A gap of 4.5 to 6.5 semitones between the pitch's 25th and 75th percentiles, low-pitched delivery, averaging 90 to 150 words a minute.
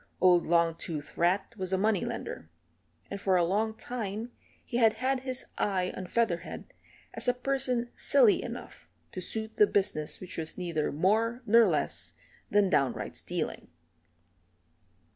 No: average, 4.9 semitones; high, 200 Hz; average, 145 wpm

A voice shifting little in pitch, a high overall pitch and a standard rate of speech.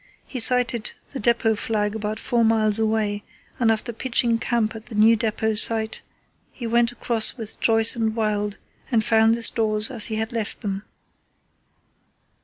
Yes: narrow, 1.4 semitones; high, 225 Hz; average, 165 wpm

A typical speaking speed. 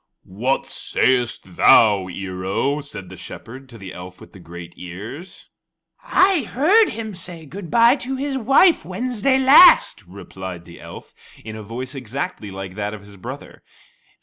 Yes: average, 160 wpm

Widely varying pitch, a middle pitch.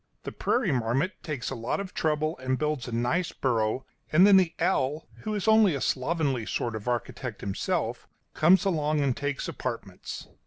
Yes: wide, 5.7 semitones; medium, 145 Hz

